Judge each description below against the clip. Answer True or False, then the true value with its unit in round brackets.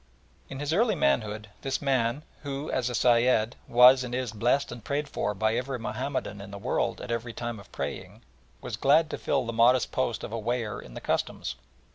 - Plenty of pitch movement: False (3.3 semitones)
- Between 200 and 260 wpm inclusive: True (205 wpm)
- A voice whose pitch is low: True (120 Hz)